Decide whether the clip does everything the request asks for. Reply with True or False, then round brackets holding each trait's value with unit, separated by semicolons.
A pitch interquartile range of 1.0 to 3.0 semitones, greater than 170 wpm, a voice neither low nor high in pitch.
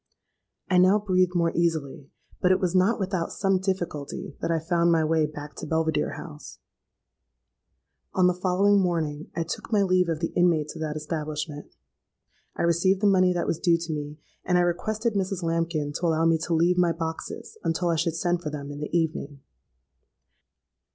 True (2.6 semitones; 185 wpm; 170 Hz)